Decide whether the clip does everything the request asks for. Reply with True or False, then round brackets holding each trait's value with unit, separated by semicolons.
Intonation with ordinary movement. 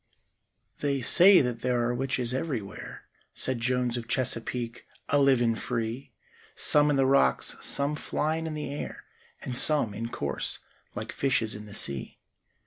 True (3.4 semitones)